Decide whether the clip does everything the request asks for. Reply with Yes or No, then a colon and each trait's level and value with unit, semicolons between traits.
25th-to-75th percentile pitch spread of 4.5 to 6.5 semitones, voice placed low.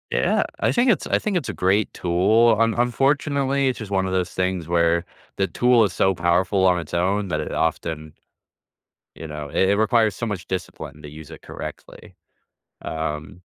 Yes: average, 5.2 semitones; very low, 95 Hz